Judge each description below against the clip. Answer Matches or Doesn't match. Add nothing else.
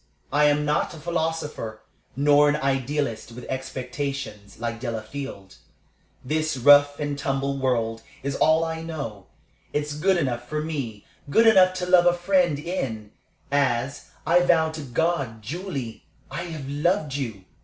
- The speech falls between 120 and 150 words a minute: Matches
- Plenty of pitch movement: Doesn't match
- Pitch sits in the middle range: Matches